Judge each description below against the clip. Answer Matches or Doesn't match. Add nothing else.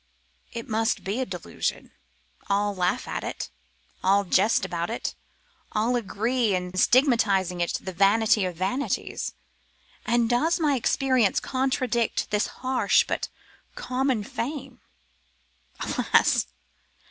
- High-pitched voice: Matches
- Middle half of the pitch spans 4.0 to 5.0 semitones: Matches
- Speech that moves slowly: Matches